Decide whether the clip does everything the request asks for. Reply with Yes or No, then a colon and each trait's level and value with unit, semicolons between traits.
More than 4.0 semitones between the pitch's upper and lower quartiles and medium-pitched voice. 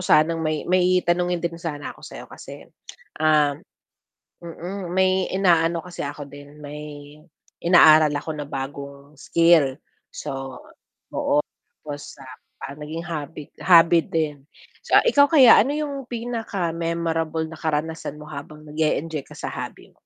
No: average, 2.9 semitones; medium, 160 Hz